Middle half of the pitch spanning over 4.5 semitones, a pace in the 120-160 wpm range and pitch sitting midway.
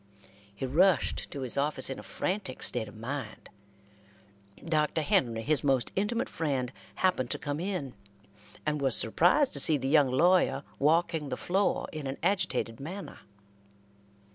Yes: average, 5.0 semitones; average, 150 wpm; medium, 145 Hz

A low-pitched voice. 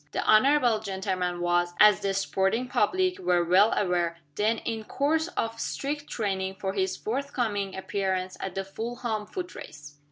No: high, 205 Hz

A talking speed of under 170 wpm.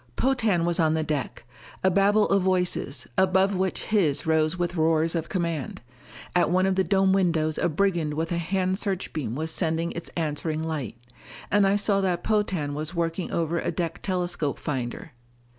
No: average, 175 wpm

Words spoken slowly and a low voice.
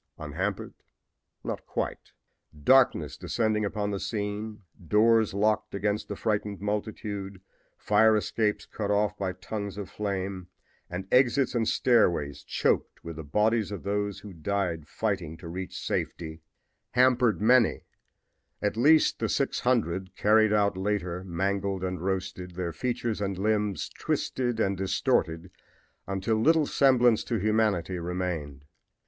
Yes: slow, 130 wpm; low, 100 Hz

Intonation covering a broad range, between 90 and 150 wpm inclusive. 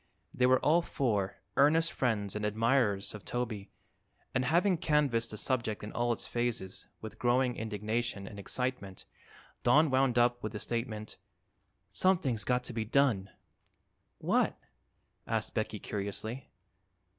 No: average, 3.5 semitones; slow, 135 wpm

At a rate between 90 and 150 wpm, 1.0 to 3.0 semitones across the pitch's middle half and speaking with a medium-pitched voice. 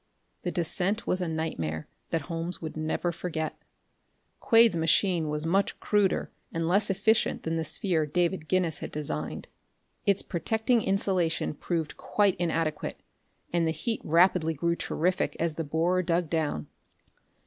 Yes: average, 145 wpm; average, 2.7 semitones; medium, 170 Hz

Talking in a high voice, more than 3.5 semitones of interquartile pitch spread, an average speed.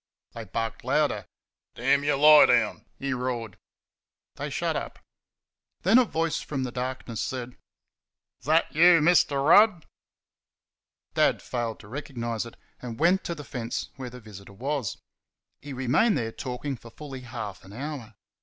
No: low, 130 Hz; average, 4.3 semitones; average, 155 wpm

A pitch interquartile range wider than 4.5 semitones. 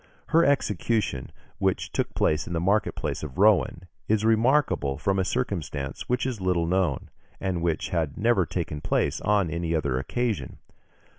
Yes: average, 5.3 semitones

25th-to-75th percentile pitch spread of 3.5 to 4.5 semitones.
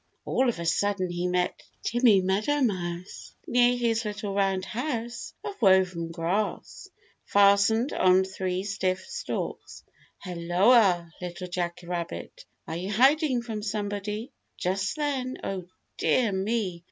Yes: average, 4.2 semitones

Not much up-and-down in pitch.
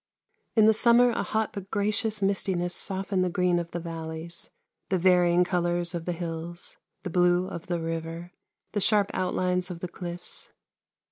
Yes: narrow, 2.1 semitones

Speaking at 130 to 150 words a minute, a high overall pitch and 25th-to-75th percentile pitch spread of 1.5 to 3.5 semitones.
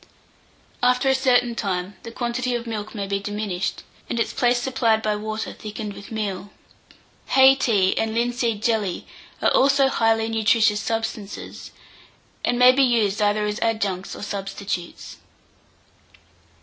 Yes: average, 140 wpm; high, 220 Hz; average, 2.8 semitones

